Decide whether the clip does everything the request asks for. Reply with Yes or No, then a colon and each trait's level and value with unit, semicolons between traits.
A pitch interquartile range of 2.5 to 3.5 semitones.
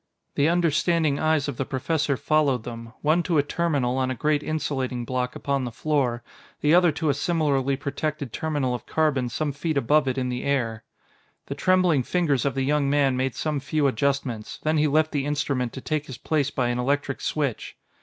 Yes: average, 3.0 semitones